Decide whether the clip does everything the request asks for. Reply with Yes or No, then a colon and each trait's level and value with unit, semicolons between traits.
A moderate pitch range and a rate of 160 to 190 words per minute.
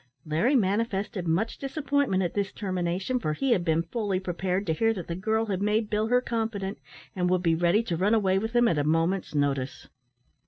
No: average, 4.5 semitones; fast, 205 wpm